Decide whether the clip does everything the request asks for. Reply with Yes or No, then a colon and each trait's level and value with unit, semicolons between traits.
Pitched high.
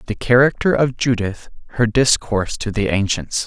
No: low, 120 Hz